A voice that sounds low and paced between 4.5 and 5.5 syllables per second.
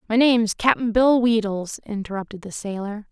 No: high, 220 Hz; 4.9 syllables/s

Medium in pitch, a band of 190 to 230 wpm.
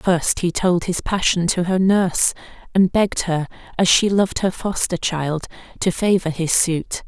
No: medium, 180 Hz; average, 180 wpm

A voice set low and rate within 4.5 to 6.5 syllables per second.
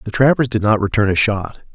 Yes: low, 110 Hz; 5.9 syllables/s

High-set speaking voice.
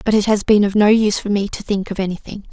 Yes: high, 205 Hz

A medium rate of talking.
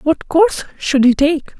Yes: average, 190 wpm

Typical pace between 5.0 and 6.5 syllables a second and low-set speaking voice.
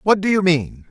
No: 5.1 syllables/s; medium, 170 Hz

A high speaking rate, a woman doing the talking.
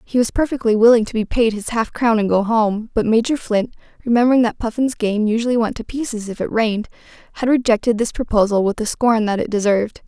Yes: fast, 220 wpm; female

